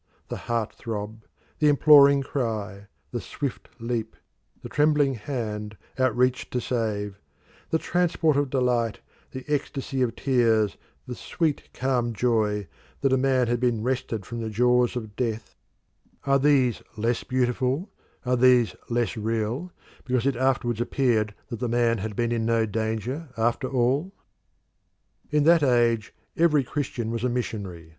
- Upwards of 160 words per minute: No, average, 150 wpm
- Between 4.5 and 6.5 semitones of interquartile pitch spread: No, average, 3.1 semitones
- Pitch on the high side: No, low, 120 Hz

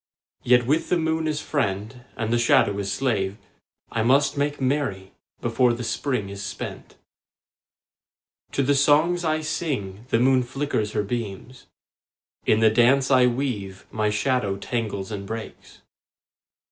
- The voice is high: No, low, 120 Hz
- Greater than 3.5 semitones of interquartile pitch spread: Yes, average, 4.9 semitones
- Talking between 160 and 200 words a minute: No, average, 145 wpm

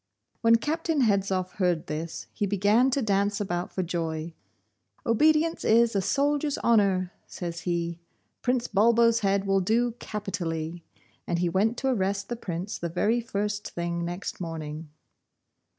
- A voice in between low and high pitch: No, high, 200 Hz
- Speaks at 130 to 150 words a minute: Yes, average, 145 wpm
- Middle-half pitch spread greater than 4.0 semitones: Yes, average, 5.0 semitones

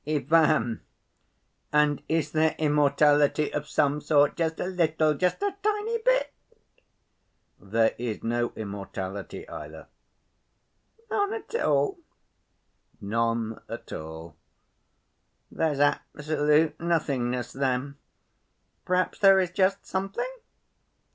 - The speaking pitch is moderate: Yes, medium, 150 Hz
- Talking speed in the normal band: No, slow, 100 wpm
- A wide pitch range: Yes, wide, 6.4 semitones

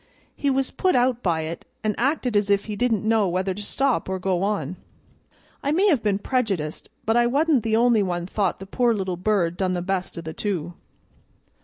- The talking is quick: Yes, fast, 210 wpm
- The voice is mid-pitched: No, high, 205 Hz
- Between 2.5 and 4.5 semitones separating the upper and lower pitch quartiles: No, average, 4.9 semitones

